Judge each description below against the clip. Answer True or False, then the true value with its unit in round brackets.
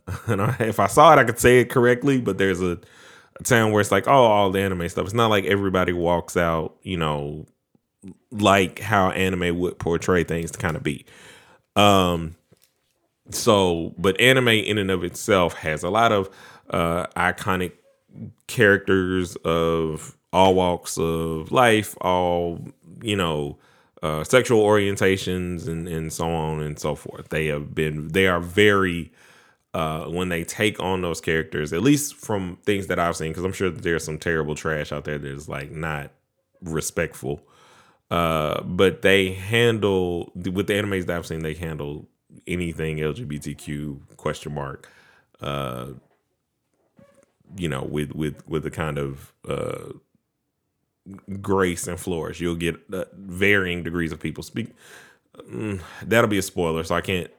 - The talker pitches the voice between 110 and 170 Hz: False (90 Hz)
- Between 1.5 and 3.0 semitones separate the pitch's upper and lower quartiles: False (3.6 semitones)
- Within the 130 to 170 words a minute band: True (160 wpm)